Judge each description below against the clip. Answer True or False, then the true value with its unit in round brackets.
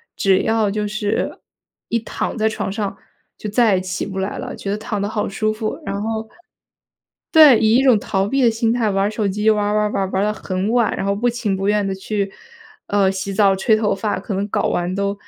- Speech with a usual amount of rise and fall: False (1.9 semitones)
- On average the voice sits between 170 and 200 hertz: False (210 Hz)